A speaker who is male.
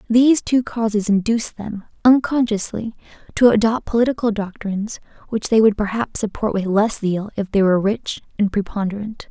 No: female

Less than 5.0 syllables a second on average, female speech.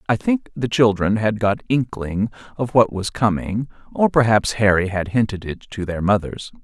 No: 4.7 syllables/s; male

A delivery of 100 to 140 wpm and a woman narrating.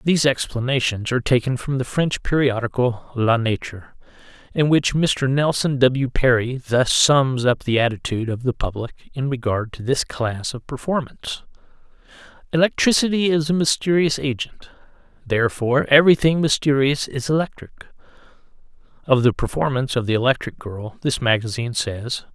No: slow, 135 wpm; male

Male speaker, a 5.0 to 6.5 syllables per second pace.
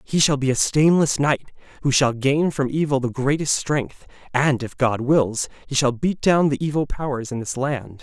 No: male; 4.6 syllables/s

